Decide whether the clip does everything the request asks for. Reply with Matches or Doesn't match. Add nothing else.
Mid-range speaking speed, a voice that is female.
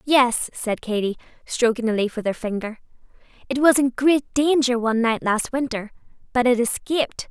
Matches